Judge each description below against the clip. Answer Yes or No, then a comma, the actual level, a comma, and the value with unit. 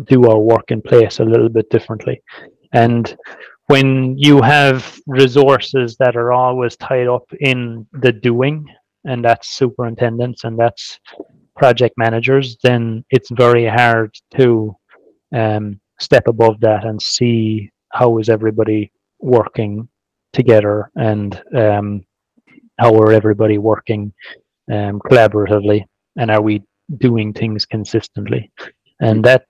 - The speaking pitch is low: Yes, low, 115 Hz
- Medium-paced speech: No, slow, 125 wpm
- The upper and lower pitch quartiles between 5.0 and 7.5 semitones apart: No, average, 2.8 semitones